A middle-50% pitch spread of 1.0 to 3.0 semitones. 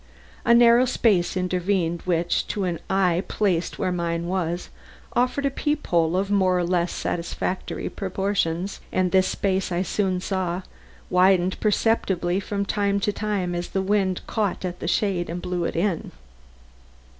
Yes: narrow, 2.4 semitones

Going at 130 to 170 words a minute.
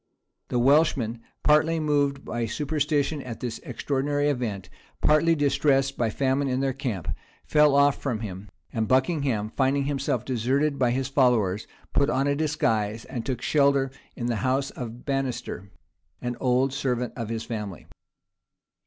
Yes: average, 150 wpm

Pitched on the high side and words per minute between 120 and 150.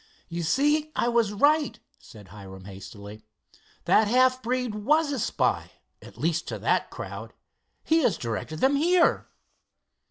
Yes: high, 230 Hz; average, 145 wpm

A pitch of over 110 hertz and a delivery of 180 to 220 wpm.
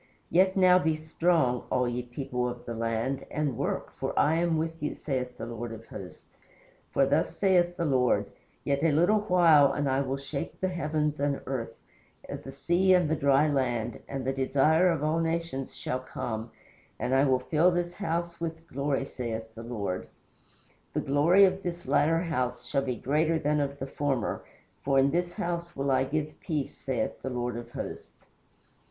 Yes: medium, 140 Hz; average, 185 wpm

